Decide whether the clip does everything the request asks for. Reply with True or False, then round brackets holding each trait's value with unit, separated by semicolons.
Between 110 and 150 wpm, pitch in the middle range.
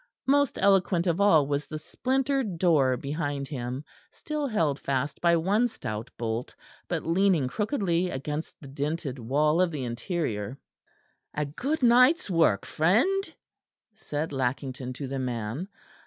True (140 wpm; 155 Hz)